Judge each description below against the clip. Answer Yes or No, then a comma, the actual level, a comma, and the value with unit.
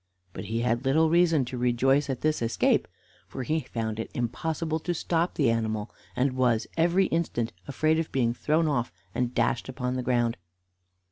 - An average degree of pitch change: Yes, average, 5.0 semitones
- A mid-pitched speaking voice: No, low, 130 Hz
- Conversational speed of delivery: Yes, average, 180 wpm